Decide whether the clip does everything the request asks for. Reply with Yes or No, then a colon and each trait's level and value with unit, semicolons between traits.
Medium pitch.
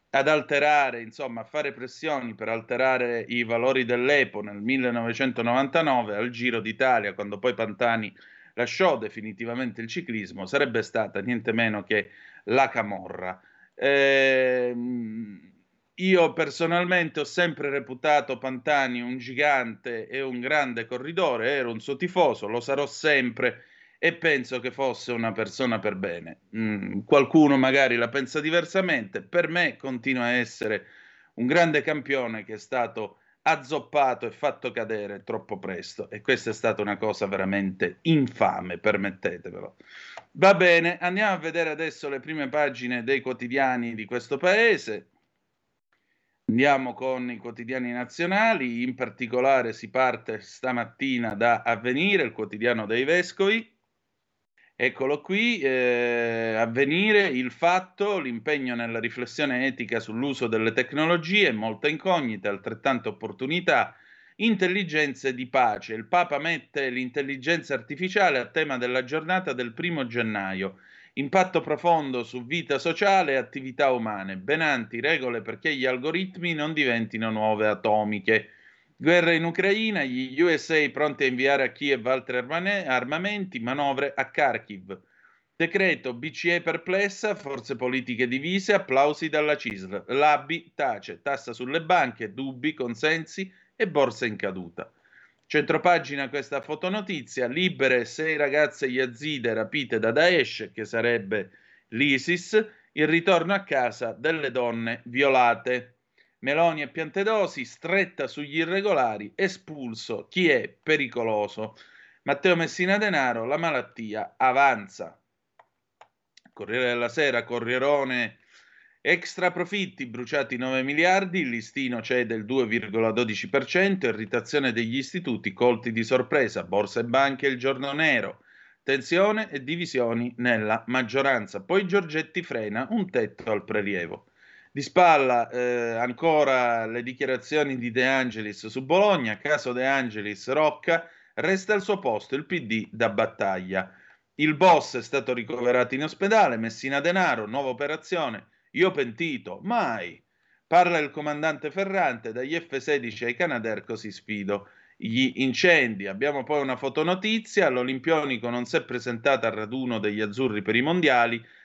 No: low, 130 Hz